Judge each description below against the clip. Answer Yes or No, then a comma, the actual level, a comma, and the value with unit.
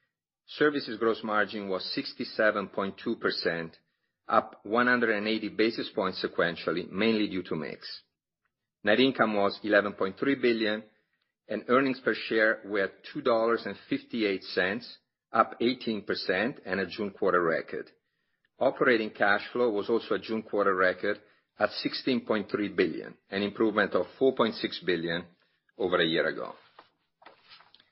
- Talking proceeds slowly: Yes, slow, 115 wpm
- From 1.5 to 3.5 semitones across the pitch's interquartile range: Yes, narrow, 2.5 semitones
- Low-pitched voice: Yes, low, 110 Hz